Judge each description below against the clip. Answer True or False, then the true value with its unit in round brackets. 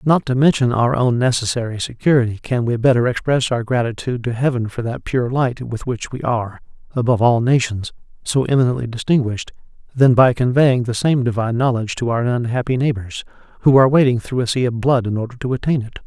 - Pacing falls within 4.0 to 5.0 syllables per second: False (6.1 syllables/s)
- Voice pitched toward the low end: True (125 Hz)